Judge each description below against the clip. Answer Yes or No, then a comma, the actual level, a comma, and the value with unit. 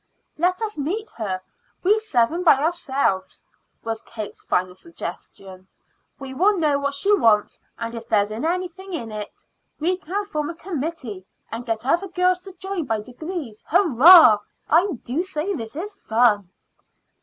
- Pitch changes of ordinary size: No, wide, 8.2 semitones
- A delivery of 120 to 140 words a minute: No, average, 160 wpm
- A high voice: Yes, very high, 300 Hz